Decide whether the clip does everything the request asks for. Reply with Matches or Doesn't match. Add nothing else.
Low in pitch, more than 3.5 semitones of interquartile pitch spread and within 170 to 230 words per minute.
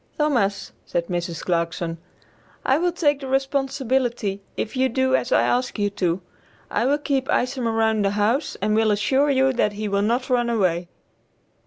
Doesn't match